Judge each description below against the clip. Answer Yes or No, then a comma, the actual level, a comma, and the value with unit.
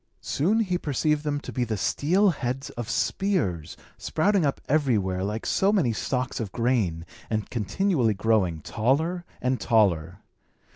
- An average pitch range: No, wide, 6.9 semitones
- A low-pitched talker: Yes, low, 125 Hz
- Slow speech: No, average, 145 wpm